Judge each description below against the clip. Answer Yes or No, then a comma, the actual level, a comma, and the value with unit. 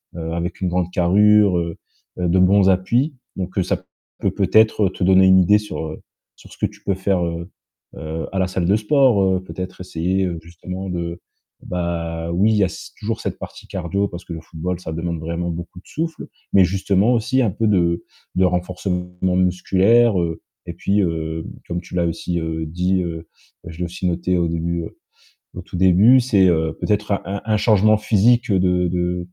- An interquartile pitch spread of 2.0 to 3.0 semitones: Yes, narrow, 2.6 semitones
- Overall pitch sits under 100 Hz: Yes, very low, 90 Hz